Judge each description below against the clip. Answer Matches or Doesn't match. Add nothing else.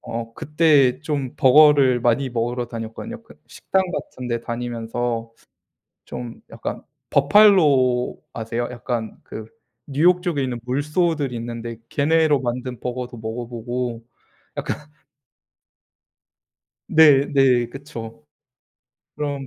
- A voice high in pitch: Doesn't match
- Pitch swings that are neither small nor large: Matches